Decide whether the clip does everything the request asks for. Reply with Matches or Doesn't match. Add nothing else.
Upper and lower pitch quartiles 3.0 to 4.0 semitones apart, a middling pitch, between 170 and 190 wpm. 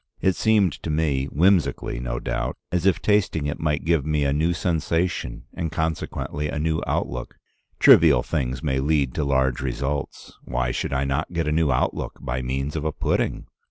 Doesn't match